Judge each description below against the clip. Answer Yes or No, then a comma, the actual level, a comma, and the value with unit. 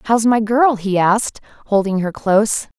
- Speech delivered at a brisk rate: No, average, 170 wpm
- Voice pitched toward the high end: Yes, high, 215 Hz